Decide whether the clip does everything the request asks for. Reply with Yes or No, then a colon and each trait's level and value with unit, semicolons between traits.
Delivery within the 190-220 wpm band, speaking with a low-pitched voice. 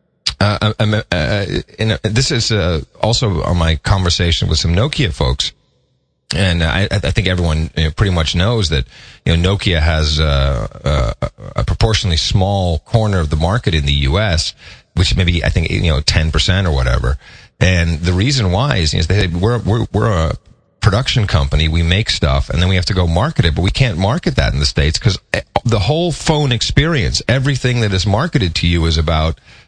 Yes: average, 200 wpm; very low, 95 Hz